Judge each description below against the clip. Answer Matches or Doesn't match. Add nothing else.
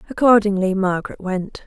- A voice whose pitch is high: Matches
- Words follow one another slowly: Matches